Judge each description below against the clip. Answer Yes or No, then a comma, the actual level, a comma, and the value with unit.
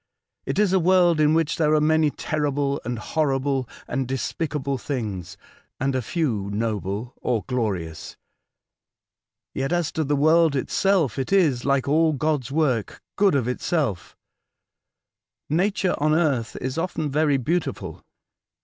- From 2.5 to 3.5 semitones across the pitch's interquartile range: No, average, 4.1 semitones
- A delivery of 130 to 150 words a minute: Yes, average, 140 wpm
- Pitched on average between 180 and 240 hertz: No, medium, 145 Hz